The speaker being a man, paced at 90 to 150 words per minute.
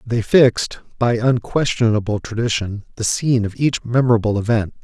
Yes: male; slow, 135 wpm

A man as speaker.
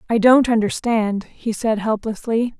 No: female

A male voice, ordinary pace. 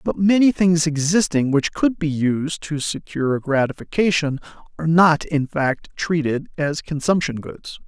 Yes: male; average, 150 wpm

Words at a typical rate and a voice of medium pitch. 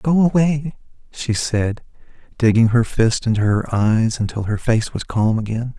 No: average, 165 wpm; low, 115 Hz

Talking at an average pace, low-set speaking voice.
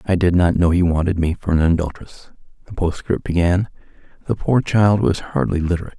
Yes: average, 190 wpm; very low, 90 Hz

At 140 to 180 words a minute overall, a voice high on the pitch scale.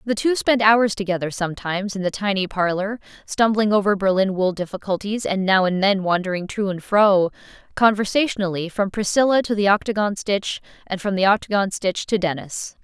Yes: average, 175 wpm; high, 200 Hz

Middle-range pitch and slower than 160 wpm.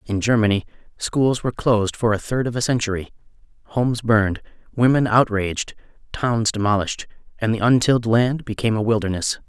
No: low, 115 Hz; average, 150 wpm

